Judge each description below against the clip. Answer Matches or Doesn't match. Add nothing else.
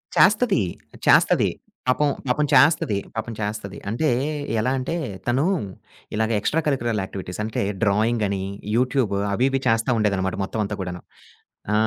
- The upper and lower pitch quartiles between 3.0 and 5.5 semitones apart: Matches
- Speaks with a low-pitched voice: Matches